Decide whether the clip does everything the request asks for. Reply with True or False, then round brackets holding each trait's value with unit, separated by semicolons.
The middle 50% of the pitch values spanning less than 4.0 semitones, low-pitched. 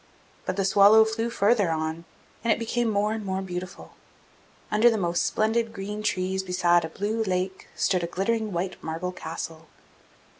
False (3.6 semitones; 195 Hz)